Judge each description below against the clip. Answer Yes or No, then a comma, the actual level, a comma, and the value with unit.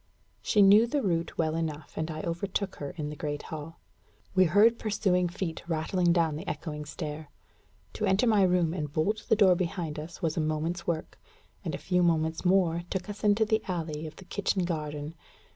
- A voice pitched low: No, medium, 170 Hz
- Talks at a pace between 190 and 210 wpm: Yes, average, 195 wpm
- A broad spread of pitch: No, average, 3.5 semitones